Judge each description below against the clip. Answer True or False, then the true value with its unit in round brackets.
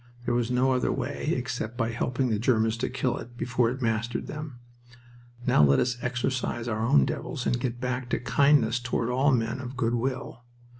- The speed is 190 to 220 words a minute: True (195 wpm)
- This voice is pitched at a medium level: False (120 Hz)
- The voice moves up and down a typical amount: False (1.8 semitones)